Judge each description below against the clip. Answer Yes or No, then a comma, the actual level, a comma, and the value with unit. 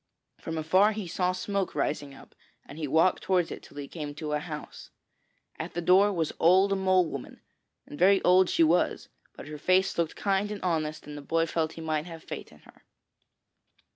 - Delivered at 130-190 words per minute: No, average, 200 wpm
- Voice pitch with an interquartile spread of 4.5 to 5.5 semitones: No, average, 3.4 semitones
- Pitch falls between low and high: Yes, medium, 165 Hz